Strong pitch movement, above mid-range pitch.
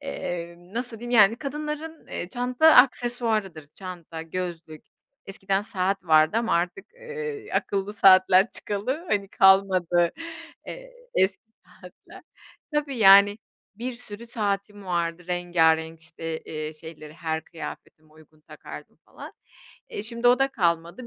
Yes: wide, 6.1 semitones; high, 195 Hz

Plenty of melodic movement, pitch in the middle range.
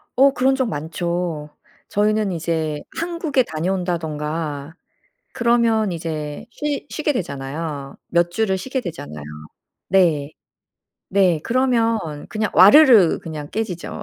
Yes: wide, 6.7 semitones; medium, 180 Hz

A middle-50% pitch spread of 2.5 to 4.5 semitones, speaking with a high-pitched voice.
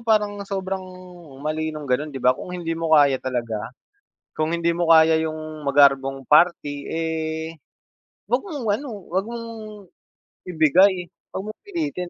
No: average, 4.2 semitones; medium, 160 Hz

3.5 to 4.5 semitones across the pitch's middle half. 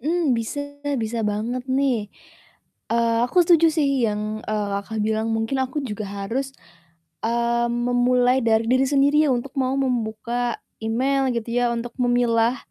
No: average, 2.8 semitones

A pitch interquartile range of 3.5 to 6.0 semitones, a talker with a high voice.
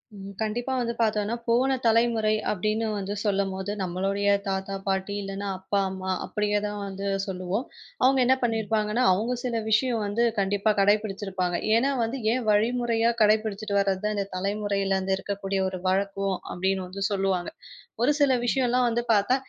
No: average, 2.7 semitones; high, 205 Hz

